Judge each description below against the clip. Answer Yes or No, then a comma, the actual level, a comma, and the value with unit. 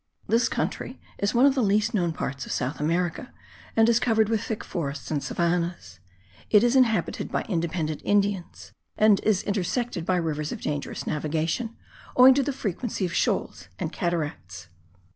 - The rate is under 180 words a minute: Yes, average, 165 wpm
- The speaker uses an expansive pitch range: Yes, wide, 5.8 semitones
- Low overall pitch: No, medium, 185 Hz